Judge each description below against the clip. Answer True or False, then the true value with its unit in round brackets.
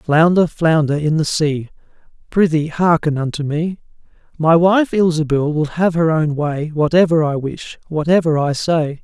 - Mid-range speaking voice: True (160 Hz)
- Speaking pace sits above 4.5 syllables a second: False (4.4 syllables/s)